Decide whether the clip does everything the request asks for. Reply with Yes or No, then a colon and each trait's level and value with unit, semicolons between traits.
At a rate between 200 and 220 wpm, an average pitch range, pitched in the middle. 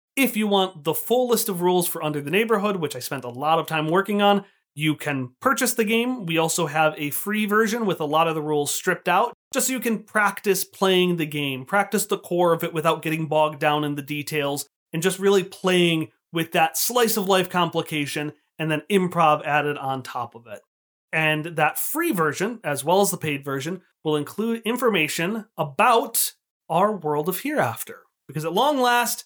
Yes: fast, 205 wpm; average, 5.0 semitones; medium, 170 Hz